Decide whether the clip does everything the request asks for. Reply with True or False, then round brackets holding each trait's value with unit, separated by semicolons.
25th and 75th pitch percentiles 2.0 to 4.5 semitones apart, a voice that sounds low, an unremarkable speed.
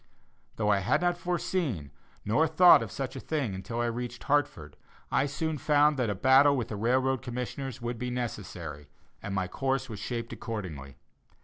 False (5.1 semitones; 120 Hz; 180 wpm)